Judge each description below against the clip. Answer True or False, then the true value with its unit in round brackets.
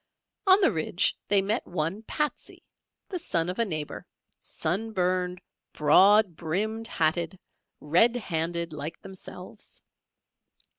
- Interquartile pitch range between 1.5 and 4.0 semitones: False (4.8 semitones)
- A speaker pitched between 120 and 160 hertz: False (180 Hz)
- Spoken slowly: True (115 wpm)